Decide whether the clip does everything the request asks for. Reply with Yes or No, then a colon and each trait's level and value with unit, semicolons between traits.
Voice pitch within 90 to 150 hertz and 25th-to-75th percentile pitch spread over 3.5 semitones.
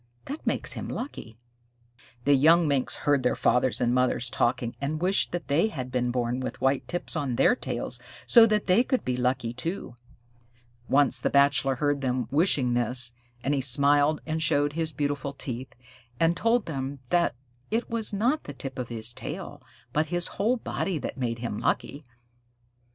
Yes: medium, 140 Hz; average, 4.9 semitones